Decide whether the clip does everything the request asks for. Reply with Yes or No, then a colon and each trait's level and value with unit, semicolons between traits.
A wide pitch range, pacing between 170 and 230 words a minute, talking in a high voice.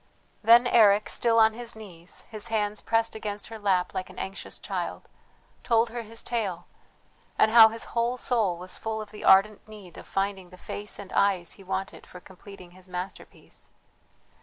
No: average, 3.1 semitones; average, 180 wpm; high, 210 Hz